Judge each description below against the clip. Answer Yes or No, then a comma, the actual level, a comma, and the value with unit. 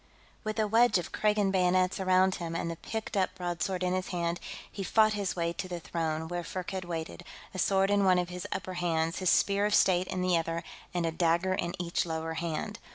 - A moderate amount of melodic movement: No, narrow, 2.1 semitones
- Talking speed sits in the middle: No, fast, 220 wpm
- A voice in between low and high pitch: Yes, medium, 180 Hz